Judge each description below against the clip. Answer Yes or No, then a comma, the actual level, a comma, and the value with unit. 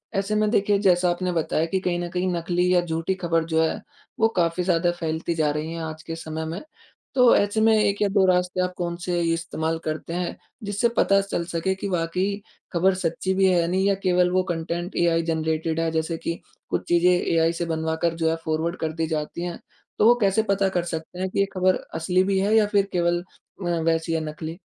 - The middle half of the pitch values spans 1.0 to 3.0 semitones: Yes, narrow, 2.5 semitones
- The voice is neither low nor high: Yes, medium, 175 Hz